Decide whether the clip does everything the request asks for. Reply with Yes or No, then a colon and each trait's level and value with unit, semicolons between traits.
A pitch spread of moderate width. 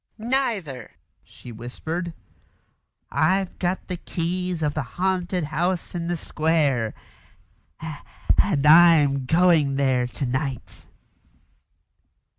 Yes: average, 4.6 semitones